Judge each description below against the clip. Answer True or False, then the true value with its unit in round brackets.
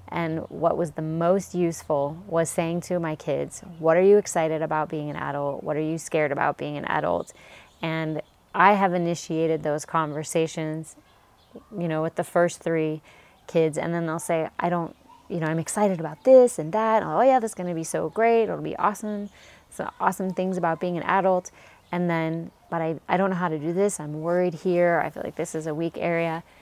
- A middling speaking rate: False (215 wpm)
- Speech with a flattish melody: True (2.2 semitones)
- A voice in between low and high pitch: True (165 Hz)